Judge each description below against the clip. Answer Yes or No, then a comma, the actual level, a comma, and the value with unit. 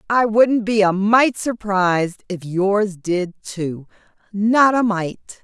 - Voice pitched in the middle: No, high, 205 Hz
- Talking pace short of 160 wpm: Yes, slow, 135 wpm